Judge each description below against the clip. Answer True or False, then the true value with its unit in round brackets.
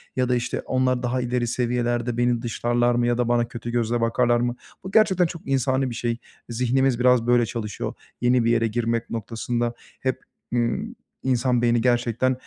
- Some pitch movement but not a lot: False (1.2 semitones)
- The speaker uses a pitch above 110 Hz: True (120 Hz)